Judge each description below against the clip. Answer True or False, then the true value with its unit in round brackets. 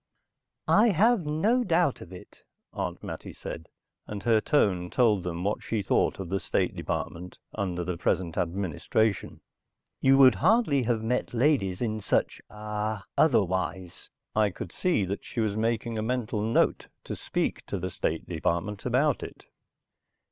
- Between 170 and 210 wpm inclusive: False (155 wpm)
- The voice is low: True (110 Hz)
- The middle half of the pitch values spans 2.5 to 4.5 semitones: False (5.4 semitones)